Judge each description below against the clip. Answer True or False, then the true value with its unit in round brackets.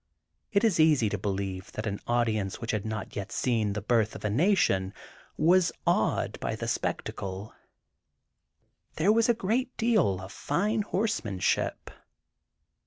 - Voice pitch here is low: True (115 Hz)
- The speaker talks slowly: False (145 wpm)